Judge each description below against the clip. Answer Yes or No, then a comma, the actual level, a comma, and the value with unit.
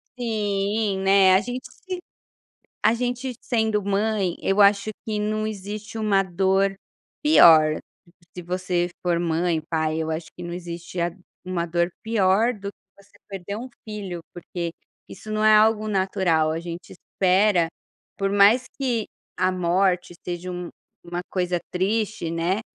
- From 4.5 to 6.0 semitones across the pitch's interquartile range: No, average, 3.5 semitones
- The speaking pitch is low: No, high, 195 Hz